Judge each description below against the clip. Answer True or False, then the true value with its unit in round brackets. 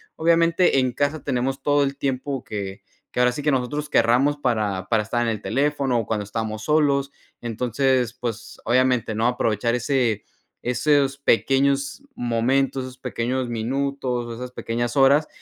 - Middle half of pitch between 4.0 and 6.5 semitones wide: False (3.0 semitones)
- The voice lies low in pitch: True (125 Hz)